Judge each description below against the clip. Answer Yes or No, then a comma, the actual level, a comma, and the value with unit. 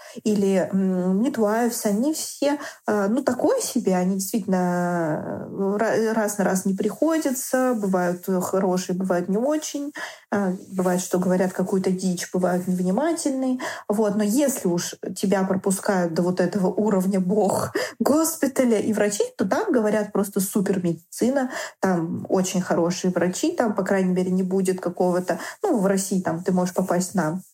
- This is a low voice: No, high, 195 Hz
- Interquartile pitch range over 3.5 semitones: Yes, average, 4.2 semitones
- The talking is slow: No, average, 145 wpm